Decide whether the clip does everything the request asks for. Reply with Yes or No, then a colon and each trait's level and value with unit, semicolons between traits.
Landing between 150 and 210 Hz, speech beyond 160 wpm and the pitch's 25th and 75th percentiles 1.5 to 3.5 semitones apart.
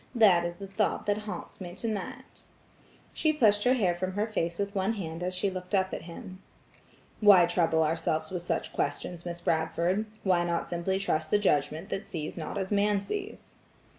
Yes: medium, 185 Hz; average, 190 wpm; average, 3.1 semitones